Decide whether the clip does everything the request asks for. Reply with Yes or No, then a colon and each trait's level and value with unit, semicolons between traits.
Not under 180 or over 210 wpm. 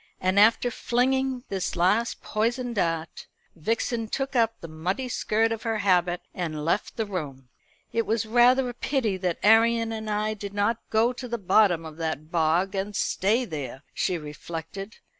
No: average, 170 wpm